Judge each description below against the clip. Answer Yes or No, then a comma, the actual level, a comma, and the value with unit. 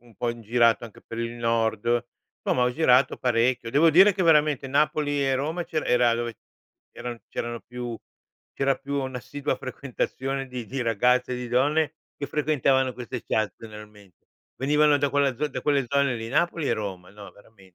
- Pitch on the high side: No, low, 125 Hz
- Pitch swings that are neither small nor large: Yes, average, 3.4 semitones